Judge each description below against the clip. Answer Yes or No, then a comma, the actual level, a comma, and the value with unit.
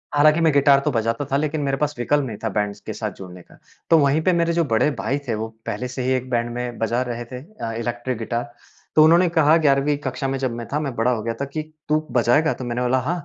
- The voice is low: Yes, low, 130 Hz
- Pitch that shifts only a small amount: No, average, 4.0 semitones